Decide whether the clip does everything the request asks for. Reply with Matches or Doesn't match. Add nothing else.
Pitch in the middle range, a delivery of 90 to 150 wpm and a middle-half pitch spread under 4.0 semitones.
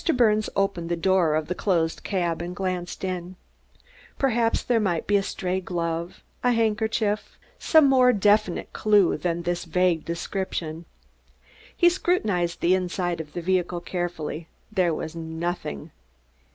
Matches